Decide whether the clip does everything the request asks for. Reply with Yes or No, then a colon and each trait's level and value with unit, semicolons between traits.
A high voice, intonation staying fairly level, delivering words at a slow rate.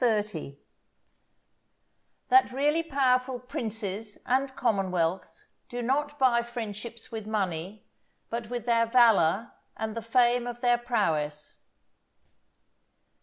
No: high, 230 Hz; average, 3.2 semitones; slow, 100 wpm